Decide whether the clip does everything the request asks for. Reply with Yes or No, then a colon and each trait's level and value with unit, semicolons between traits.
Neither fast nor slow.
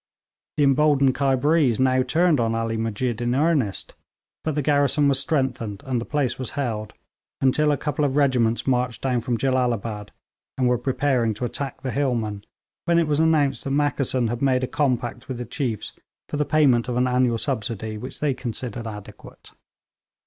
Yes: average, 180 wpm